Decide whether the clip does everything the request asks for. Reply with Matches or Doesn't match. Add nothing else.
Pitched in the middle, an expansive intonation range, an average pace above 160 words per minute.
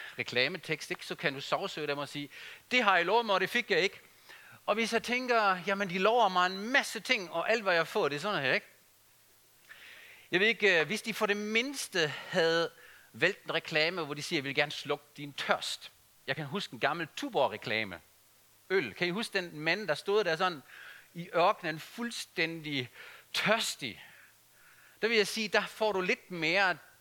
Matches